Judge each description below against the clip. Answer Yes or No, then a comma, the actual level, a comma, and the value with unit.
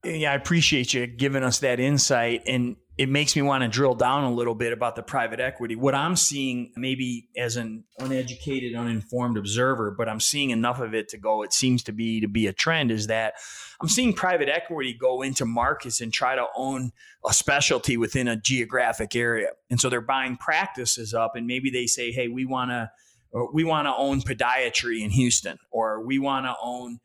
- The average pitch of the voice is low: Yes, low, 125 Hz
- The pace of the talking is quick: Yes, fast, 210 wpm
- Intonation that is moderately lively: No, narrow, 2.3 semitones